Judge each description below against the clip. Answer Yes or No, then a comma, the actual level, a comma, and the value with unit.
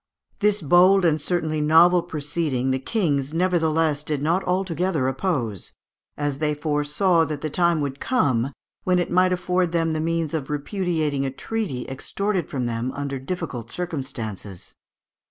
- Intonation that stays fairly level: No, average, 4.3 semitones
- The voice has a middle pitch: Yes, medium, 155 Hz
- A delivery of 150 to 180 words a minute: Yes, average, 155 wpm